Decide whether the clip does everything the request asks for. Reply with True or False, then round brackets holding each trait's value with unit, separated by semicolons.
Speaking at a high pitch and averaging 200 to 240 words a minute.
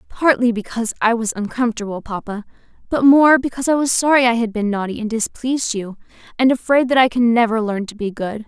True (235 Hz; 205 wpm)